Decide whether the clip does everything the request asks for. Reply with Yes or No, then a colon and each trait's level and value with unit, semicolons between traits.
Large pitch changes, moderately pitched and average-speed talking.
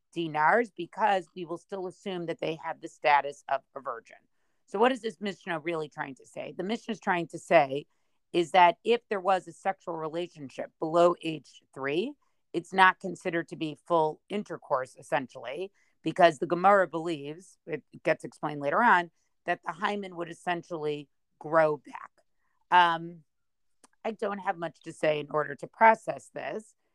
No: average, 3.3 semitones; medium, 170 Hz; average, 170 wpm